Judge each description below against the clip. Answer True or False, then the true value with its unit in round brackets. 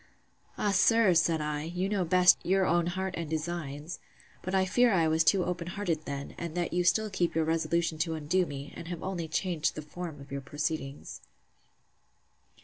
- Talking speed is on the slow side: False (190 wpm)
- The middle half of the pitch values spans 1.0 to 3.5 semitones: True (2.9 semitones)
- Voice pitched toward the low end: False (170 Hz)